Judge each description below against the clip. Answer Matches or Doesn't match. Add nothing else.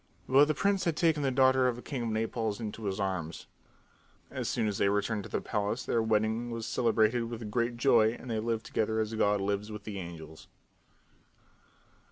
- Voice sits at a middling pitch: Doesn't match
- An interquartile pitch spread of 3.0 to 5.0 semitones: Doesn't match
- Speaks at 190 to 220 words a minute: Matches